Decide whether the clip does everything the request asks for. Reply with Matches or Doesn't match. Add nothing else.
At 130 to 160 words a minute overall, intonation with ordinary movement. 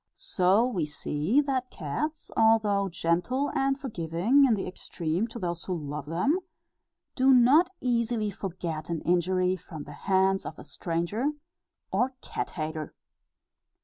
Doesn't match